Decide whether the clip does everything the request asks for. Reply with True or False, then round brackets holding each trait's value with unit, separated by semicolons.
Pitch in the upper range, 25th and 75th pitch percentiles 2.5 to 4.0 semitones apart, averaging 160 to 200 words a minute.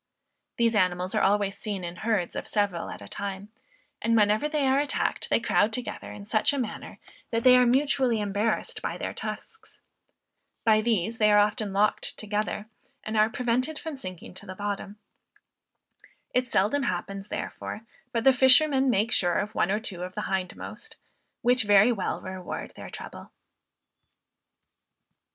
True (215 Hz; 3.7 semitones; 165 wpm)